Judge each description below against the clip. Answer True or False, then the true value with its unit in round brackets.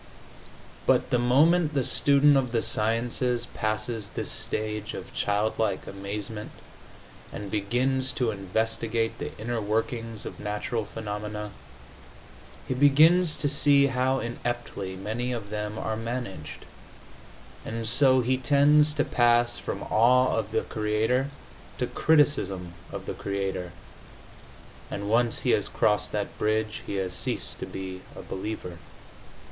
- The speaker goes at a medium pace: False (130 wpm)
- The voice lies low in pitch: True (115 Hz)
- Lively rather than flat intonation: False (3.4 semitones)